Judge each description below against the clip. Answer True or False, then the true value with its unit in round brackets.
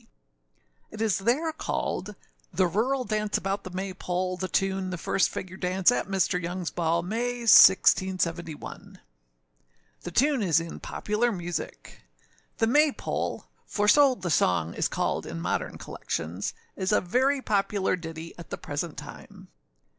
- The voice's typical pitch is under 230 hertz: True (190 Hz)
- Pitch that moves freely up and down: False (3.9 semitones)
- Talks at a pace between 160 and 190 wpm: False (150 wpm)